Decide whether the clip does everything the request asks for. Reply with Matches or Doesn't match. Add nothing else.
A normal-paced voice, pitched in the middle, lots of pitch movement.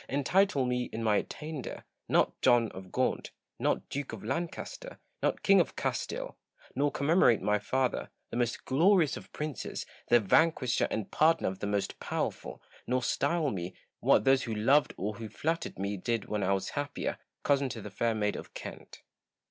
Doesn't match